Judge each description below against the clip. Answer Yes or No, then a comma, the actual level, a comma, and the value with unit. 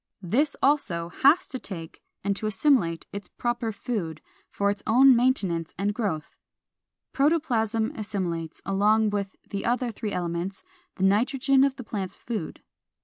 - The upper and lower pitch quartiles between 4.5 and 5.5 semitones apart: Yes, average, 4.8 semitones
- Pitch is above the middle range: Yes, high, 210 Hz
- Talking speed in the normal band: Yes, average, 145 wpm